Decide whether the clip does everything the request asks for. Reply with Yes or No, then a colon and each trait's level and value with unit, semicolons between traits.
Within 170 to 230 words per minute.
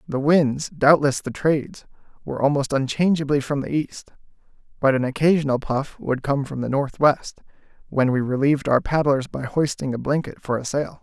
Yes: average, 175 wpm